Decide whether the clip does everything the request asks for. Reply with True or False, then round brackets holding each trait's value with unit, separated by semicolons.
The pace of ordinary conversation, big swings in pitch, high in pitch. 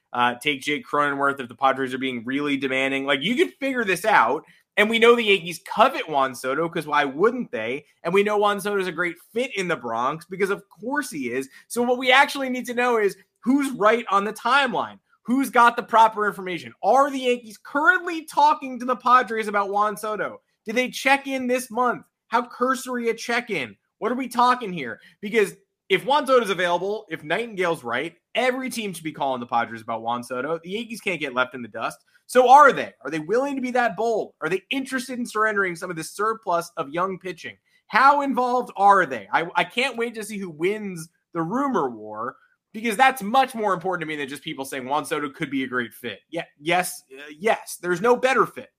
False (225 wpm; 7.5 semitones; 205 Hz)